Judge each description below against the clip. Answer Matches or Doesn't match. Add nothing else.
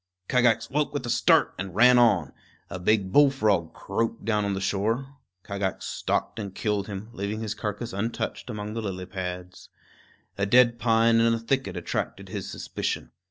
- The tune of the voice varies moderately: Matches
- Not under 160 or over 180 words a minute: Matches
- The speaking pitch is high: Doesn't match